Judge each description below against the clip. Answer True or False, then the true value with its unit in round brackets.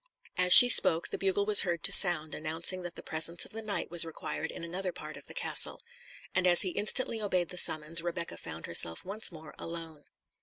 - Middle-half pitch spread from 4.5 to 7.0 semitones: False (2.9 semitones)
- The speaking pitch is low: False (175 Hz)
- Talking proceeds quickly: True (215 wpm)